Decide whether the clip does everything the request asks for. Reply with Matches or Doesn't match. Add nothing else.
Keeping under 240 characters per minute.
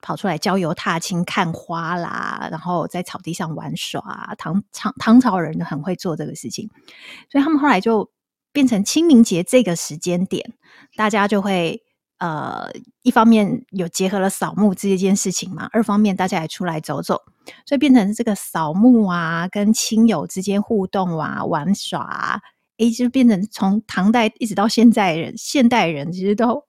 Doesn't match